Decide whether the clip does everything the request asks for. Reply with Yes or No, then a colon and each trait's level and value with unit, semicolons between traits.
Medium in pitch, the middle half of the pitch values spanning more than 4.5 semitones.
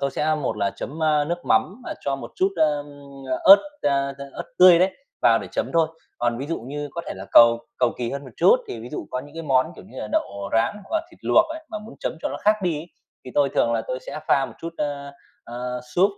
Yes: medium, 145 Hz; average, 5.1 semitones